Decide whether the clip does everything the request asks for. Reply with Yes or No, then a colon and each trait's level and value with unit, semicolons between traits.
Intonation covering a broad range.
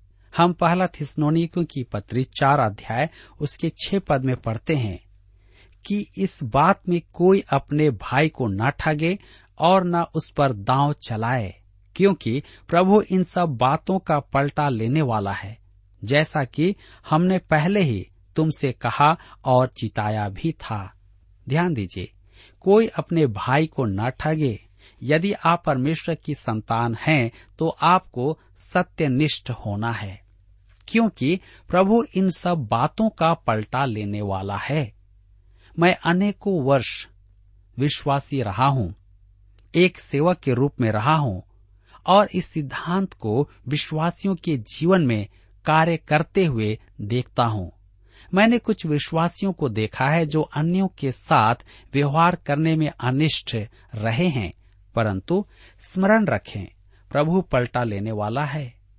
Yes: wide, 7.8 semitones